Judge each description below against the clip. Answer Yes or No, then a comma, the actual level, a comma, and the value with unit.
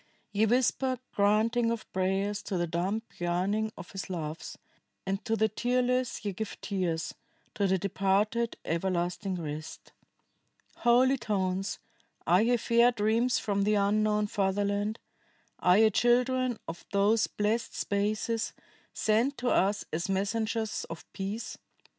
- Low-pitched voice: No, high, 210 Hz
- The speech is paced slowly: Yes, slow, 130 wpm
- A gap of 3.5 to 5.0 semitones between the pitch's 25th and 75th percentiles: No, average, 3.1 semitones